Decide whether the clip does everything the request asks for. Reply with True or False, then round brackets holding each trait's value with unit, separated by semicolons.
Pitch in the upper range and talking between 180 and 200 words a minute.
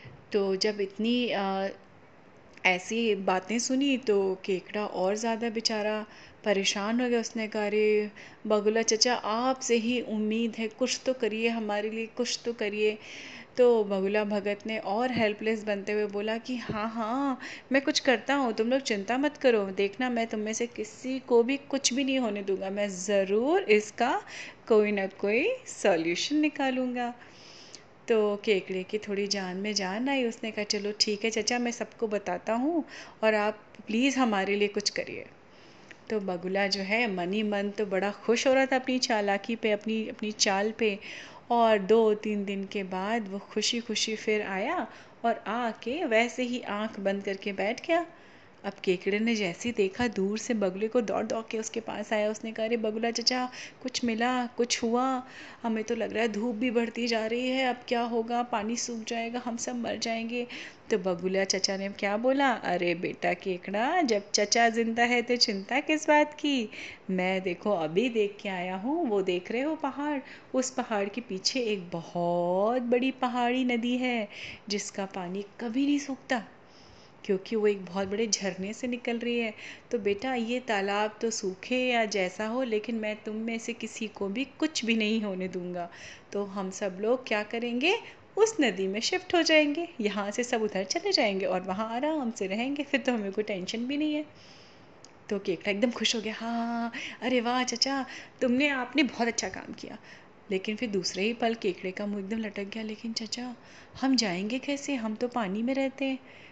True (225 Hz; 185 wpm)